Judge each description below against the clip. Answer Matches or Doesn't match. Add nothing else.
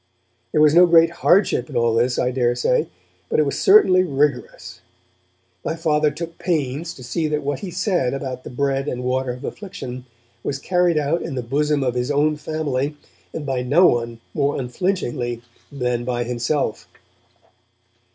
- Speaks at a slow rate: Doesn't match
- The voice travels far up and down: Doesn't match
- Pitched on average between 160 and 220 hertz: Doesn't match